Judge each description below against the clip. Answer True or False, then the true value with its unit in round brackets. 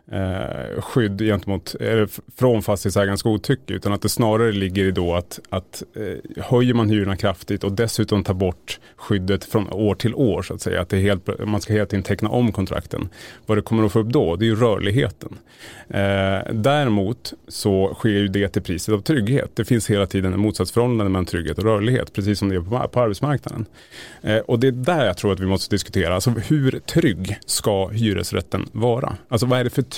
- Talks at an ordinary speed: False (200 wpm)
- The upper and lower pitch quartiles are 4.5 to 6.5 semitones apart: False (3.1 semitones)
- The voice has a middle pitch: False (105 Hz)